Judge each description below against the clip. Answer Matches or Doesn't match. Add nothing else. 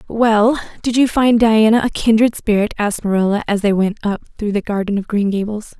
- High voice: Matches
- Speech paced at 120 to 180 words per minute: Doesn't match